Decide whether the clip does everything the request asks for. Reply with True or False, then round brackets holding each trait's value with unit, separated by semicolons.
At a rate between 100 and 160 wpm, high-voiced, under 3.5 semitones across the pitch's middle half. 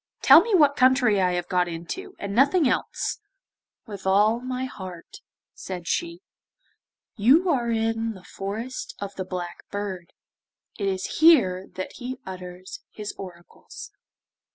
False (140 wpm; 205 Hz; 5.6 semitones)